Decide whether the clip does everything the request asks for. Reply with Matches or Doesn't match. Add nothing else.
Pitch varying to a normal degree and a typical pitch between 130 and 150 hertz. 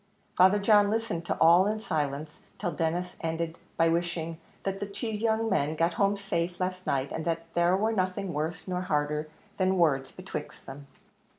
Doesn't match